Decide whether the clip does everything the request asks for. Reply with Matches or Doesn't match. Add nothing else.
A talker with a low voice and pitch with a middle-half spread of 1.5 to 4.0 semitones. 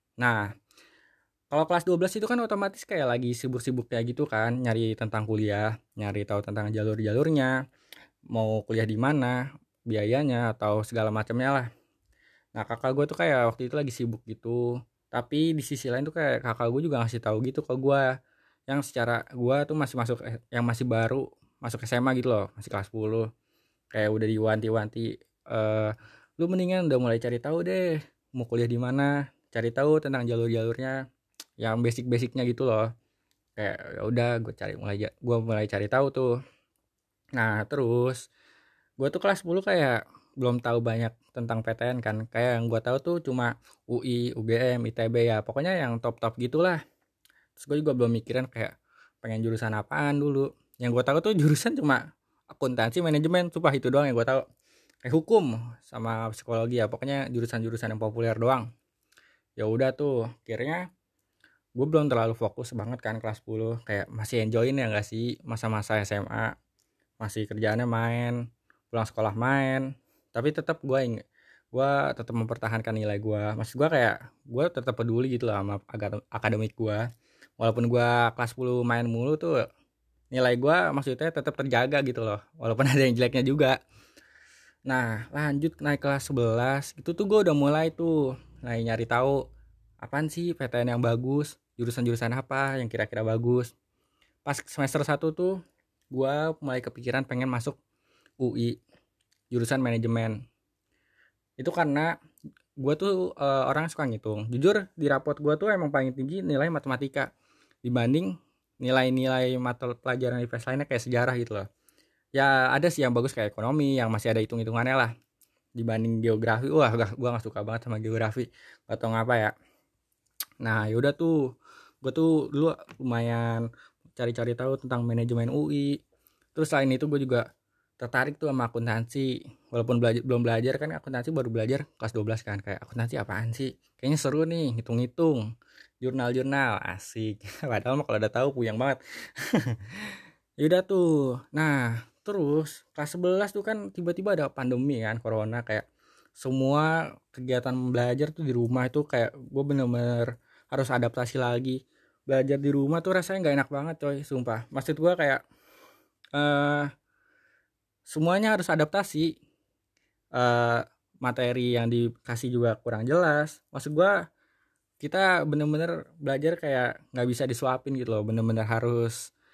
Matches